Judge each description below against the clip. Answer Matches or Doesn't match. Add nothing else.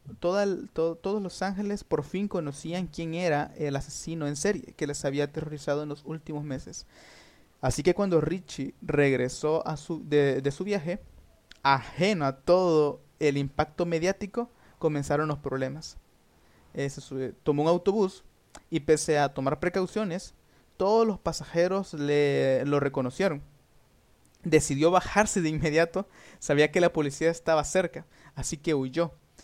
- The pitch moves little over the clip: Doesn't match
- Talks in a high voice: Doesn't match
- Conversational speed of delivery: Matches